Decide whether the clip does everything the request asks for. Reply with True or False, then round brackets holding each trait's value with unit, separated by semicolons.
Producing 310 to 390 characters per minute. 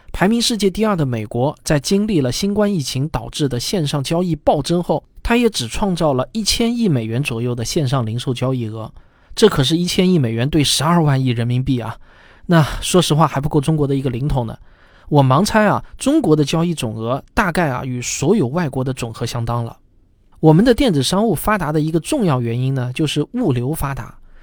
True (315 characters per minute)